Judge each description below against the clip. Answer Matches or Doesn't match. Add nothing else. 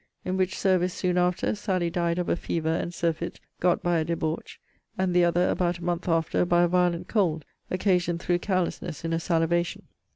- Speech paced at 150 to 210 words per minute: Matches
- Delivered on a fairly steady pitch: Matches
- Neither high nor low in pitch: Matches